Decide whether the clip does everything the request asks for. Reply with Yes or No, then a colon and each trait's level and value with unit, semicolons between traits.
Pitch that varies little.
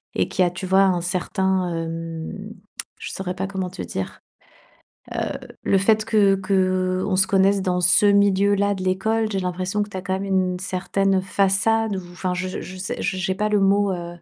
Yes: narrow, 1.5 semitones